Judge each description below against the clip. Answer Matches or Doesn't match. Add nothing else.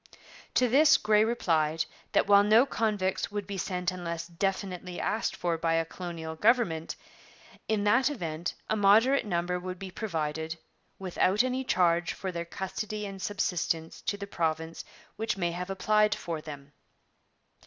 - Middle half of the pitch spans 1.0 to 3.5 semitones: Doesn't match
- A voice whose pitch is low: Doesn't match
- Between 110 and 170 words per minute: Matches